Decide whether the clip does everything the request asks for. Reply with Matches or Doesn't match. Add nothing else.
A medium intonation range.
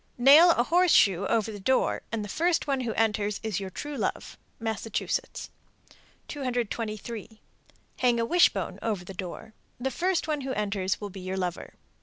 Matches